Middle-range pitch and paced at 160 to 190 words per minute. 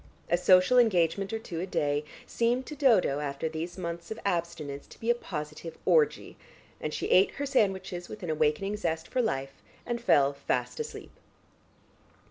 Yes: medium, 180 Hz; average, 170 wpm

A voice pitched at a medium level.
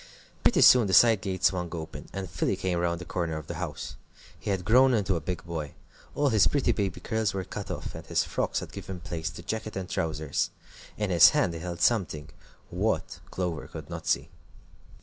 No: very low, 90 Hz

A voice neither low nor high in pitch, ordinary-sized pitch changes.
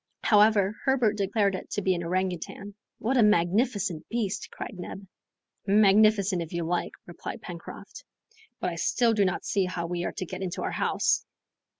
No: high, 195 Hz; average, 3.1 semitones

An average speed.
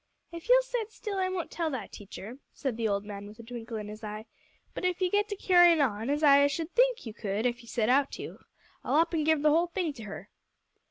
No: fast, 255 wpm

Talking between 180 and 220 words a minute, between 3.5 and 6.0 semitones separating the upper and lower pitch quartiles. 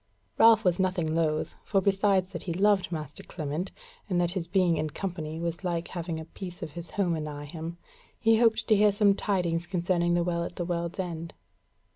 No: average, 200 wpm; narrow, 2.4 semitones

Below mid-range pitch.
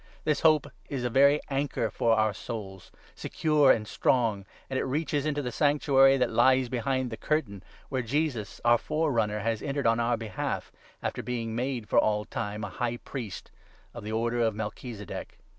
Yes: low, 120 Hz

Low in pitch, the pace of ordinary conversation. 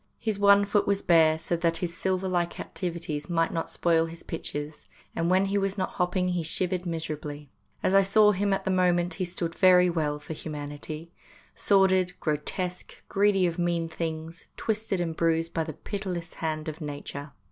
No: medium, 175 Hz; average, 180 wpm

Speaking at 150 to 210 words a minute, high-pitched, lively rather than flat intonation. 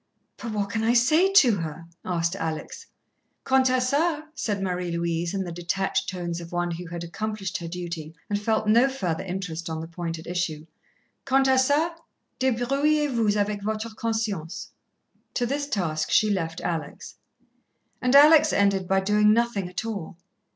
Yes: average, 170 wpm; high, 200 Hz; wide, 6.1 semitones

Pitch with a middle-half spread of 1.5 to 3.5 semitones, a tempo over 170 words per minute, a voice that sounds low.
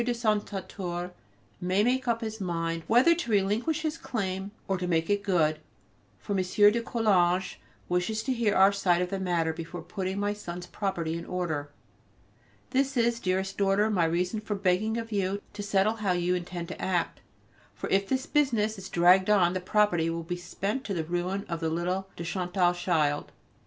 No: average, 3.2 semitones; average, 190 wpm; high, 190 Hz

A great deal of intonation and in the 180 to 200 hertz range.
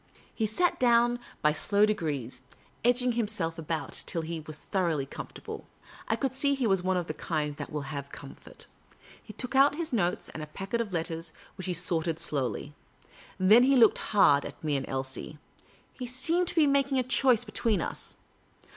Yes: wide, 7.9 semitones; high, 190 Hz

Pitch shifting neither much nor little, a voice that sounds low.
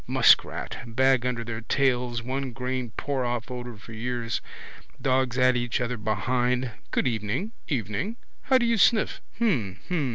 No: narrow, 2.1 semitones; low, 125 Hz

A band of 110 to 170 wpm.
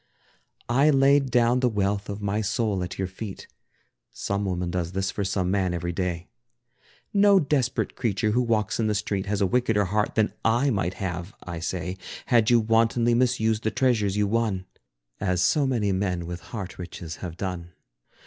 No: average, 180 wpm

